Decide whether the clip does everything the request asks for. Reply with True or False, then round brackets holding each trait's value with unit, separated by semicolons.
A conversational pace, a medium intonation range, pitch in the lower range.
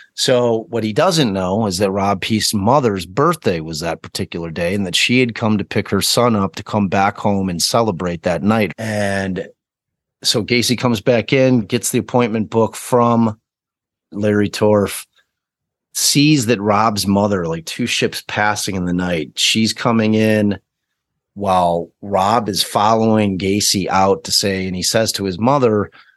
True (170 wpm; 3.0 semitones; 105 Hz)